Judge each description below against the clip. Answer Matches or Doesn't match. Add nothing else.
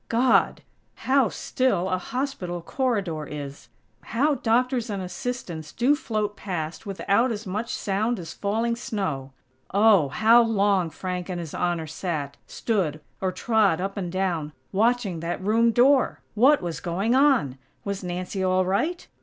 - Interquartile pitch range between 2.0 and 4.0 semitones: Doesn't match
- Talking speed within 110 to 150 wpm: Matches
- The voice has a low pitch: Doesn't match